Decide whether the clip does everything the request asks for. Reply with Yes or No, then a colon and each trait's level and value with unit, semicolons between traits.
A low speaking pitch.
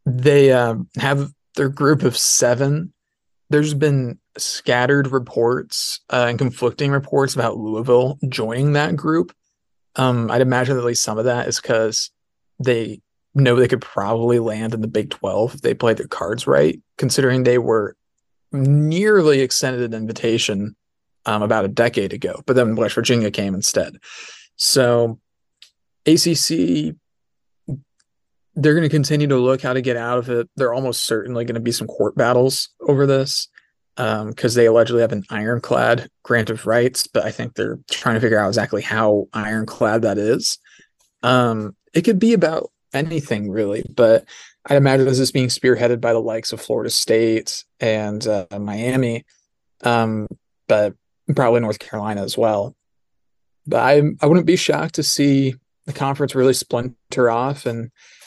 Yes: low, 125 Hz